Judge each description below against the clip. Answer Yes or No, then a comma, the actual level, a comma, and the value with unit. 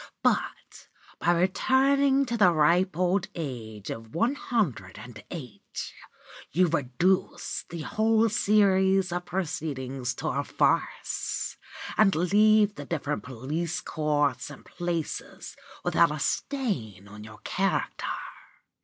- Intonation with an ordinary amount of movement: No, wide, 6.9 semitones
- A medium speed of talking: No, slow, 120 wpm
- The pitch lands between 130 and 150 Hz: No, medium, 175 Hz